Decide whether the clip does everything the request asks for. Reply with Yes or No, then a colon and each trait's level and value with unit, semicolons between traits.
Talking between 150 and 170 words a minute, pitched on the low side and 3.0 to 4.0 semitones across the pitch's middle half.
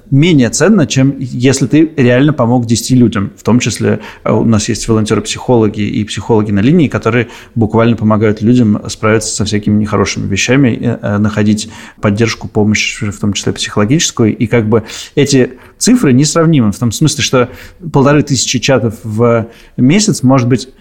Yes: average, 155 wpm; low, 115 Hz; average, 3.4 semitones